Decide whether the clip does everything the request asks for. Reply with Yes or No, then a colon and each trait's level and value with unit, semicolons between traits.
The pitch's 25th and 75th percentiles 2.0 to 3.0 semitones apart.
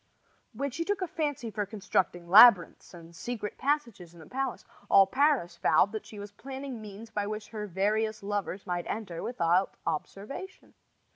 No: average, 4.9 semitones